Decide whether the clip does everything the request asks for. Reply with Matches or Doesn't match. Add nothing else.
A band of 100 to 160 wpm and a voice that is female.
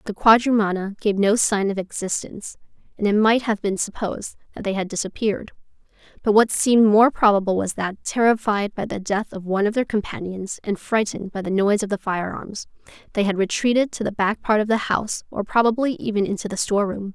Doesn't match